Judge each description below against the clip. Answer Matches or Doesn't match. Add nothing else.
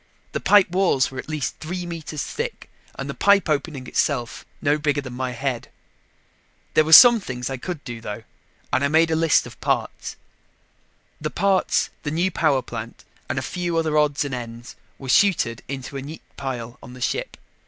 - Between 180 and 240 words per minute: Matches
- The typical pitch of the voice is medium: Matches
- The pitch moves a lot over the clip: Doesn't match